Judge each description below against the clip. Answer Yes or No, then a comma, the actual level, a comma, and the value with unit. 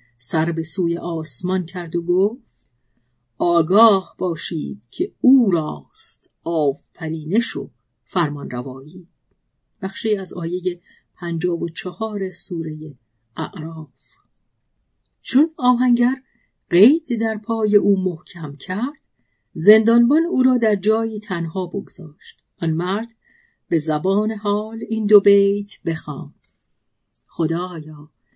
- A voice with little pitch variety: No, average, 5.2 semitones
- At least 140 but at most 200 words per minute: No, slow, 105 wpm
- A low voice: No, medium, 180 Hz